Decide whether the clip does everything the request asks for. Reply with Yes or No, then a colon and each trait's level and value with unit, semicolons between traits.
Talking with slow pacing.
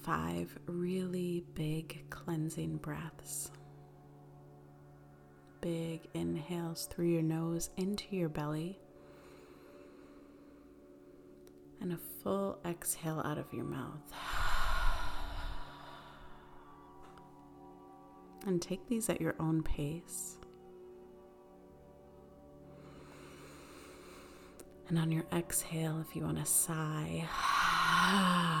Yes: slow, 80 wpm